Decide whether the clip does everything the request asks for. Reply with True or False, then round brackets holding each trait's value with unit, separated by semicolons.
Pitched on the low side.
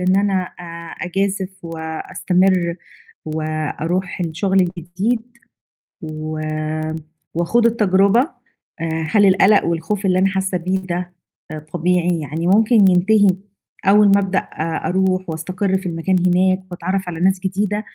False (185 Hz)